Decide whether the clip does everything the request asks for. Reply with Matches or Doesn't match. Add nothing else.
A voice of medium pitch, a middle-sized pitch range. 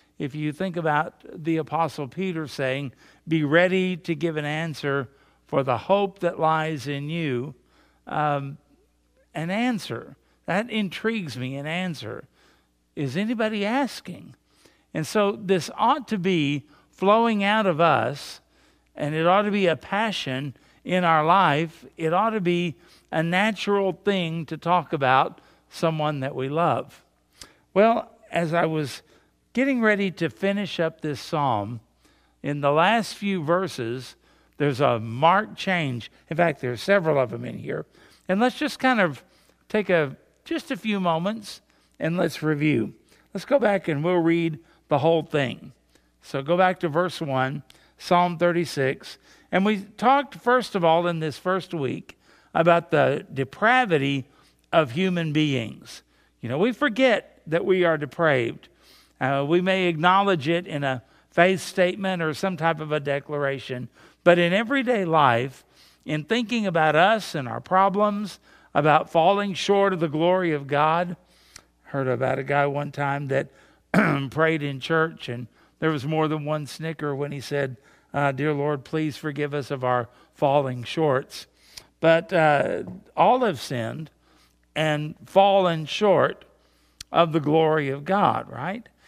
Matches